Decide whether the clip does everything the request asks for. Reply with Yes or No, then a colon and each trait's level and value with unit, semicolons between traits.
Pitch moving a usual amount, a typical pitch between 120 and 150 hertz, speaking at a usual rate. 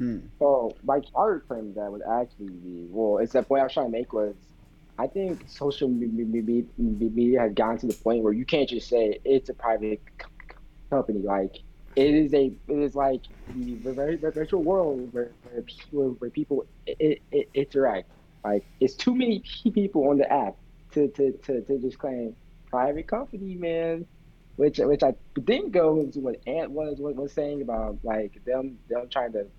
Yes: average, 4.9 semitones; low, 135 Hz; average, 185 wpm